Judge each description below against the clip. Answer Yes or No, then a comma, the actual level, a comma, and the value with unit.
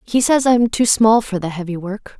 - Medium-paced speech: No, fast, 245 wpm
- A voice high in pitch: Yes, high, 215 Hz